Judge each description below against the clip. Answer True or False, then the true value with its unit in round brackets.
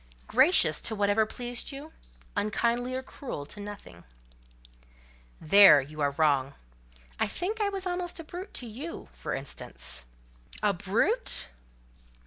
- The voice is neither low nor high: False (230 Hz)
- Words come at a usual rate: False (125 wpm)